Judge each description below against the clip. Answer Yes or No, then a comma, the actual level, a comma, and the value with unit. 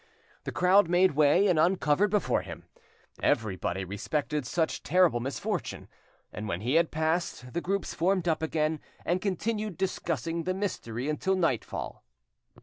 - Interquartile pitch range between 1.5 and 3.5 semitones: No, average, 4.4 semitones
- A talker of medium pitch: Yes, medium, 165 Hz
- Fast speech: No, average, 145 wpm